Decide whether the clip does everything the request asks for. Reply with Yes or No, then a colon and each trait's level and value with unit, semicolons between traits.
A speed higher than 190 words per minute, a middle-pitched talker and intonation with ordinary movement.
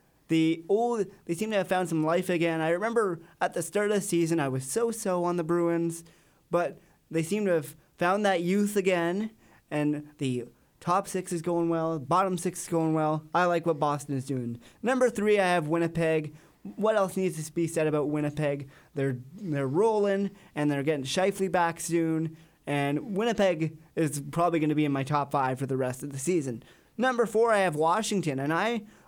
Yes: average, 200 wpm; medium, 170 Hz; average, 4.0 semitones